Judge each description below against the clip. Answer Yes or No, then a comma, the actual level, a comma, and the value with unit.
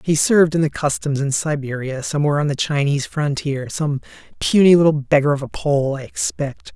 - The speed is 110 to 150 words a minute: No, average, 185 wpm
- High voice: No, medium, 145 Hz